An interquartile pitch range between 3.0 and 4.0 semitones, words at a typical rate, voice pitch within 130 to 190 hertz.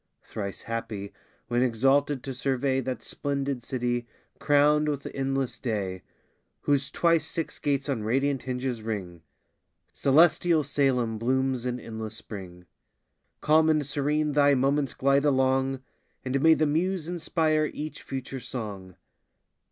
No: average, 3.3 semitones; slow, 130 wpm; low, 135 Hz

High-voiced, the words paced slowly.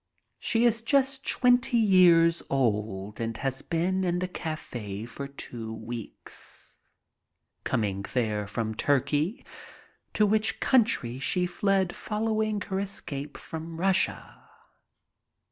No: medium, 165 Hz; slow, 110 wpm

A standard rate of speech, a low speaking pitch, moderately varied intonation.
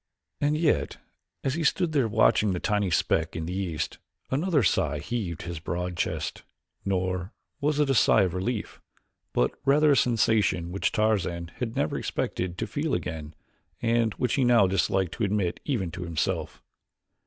No: average, 165 wpm; low, 100 Hz; wide, 6.1 semitones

